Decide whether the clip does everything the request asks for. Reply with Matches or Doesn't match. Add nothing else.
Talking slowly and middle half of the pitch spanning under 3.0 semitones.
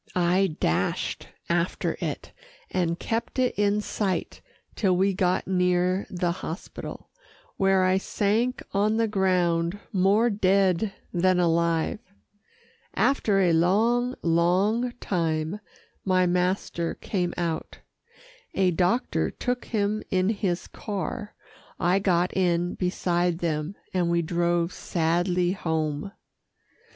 Matches